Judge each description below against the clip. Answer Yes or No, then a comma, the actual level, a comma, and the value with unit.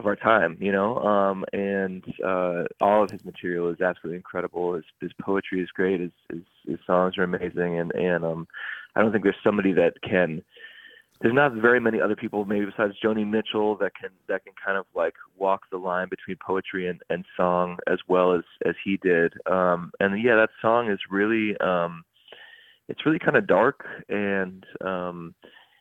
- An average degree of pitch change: Yes, average, 3.1 semitones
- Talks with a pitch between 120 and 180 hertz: No, very low, 95 Hz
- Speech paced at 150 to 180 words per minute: No, average, 190 wpm